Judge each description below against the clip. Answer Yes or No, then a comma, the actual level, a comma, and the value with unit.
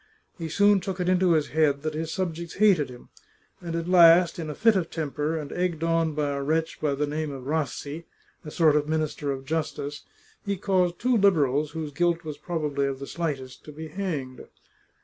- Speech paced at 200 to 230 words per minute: Yes, fast, 205 wpm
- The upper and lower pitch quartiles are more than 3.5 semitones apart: No, average, 2.9 semitones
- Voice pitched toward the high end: No, medium, 160 Hz